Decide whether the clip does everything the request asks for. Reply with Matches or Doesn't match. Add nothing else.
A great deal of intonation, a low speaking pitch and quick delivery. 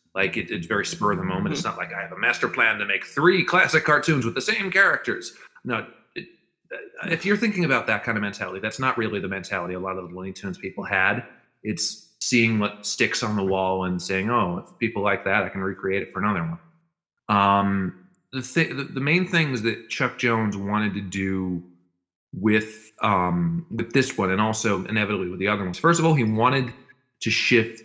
Matches